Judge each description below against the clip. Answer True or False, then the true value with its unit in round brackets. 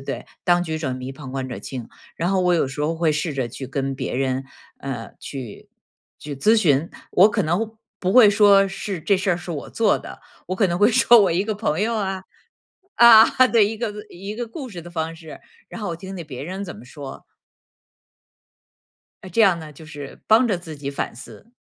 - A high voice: False (175 Hz)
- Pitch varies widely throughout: True (6.3 semitones)